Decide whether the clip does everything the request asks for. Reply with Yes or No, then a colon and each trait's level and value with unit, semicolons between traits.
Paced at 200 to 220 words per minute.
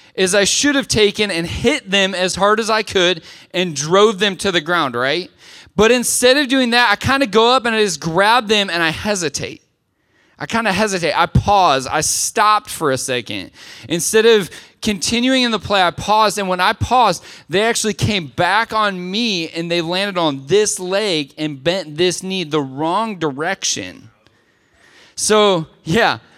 No: average, 185 wpm